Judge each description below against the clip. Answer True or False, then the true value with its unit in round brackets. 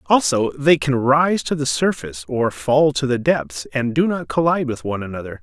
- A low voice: True (130 Hz)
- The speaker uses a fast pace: True (210 wpm)